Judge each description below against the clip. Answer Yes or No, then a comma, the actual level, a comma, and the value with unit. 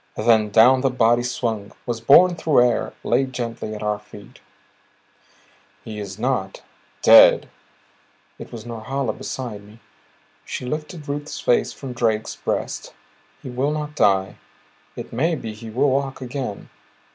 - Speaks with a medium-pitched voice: No, low, 120 Hz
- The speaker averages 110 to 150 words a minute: Yes, average, 145 wpm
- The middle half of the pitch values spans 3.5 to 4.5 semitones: Yes, average, 3.8 semitones